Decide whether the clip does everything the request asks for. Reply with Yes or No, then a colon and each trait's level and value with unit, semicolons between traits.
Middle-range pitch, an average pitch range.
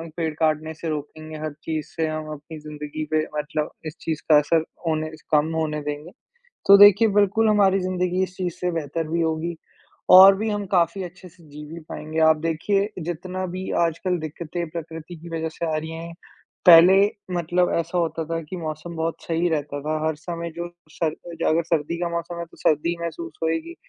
No: medium, 165 Hz; narrow, 2.2 semitones